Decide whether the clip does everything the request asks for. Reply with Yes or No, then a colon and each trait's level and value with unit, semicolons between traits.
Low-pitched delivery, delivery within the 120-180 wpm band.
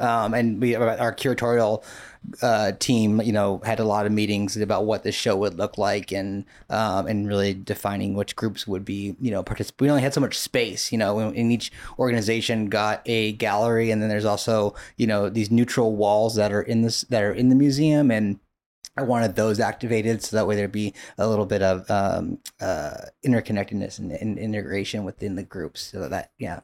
No: low, 110 Hz; fast, 205 wpm